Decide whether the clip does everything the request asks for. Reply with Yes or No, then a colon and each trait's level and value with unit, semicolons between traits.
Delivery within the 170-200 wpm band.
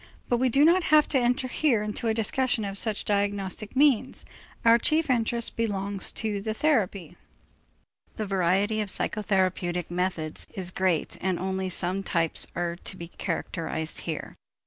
No: average, 160 wpm